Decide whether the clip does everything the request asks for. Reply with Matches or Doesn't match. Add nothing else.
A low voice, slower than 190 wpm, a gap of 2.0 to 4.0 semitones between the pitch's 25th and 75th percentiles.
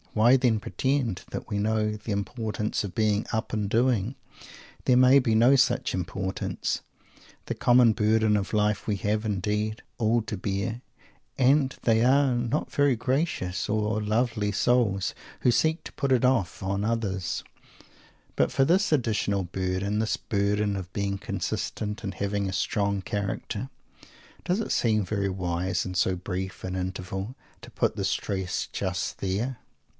Matches